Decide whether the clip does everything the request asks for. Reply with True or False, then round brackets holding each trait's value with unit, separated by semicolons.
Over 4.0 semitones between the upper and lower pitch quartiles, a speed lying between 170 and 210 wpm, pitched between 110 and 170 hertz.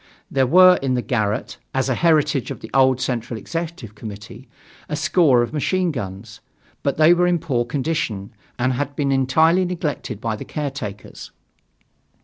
False (5.1 semitones; 160 wpm; 135 Hz)